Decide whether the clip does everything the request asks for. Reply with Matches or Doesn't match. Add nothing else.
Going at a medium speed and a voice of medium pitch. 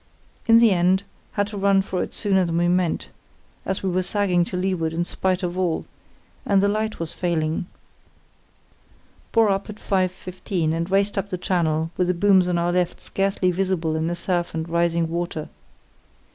Matches